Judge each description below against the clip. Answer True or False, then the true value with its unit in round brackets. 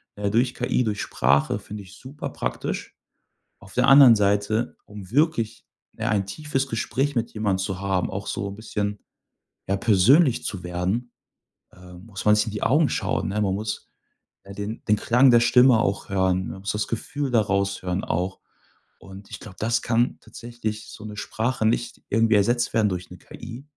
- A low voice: True (105 Hz)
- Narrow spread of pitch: False (3.3 semitones)